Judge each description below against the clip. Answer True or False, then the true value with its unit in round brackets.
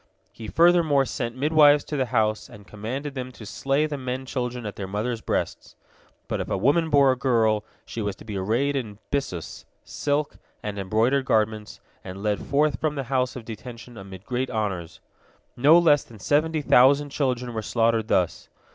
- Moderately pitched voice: False (125 Hz)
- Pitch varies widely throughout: False (4.6 semitones)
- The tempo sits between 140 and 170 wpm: False (180 wpm)